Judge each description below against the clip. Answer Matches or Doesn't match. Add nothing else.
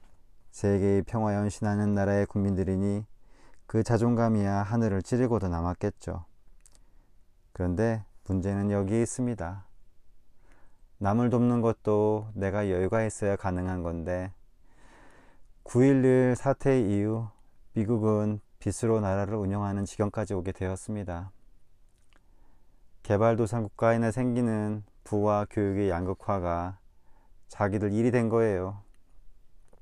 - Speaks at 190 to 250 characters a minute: Matches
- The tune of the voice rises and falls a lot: Doesn't match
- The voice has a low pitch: Matches